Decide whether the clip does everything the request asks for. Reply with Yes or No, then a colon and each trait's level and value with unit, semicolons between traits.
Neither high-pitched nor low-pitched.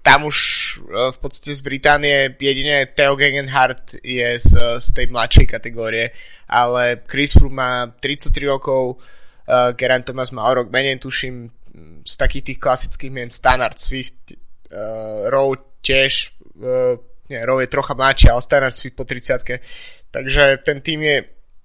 No: low, 130 Hz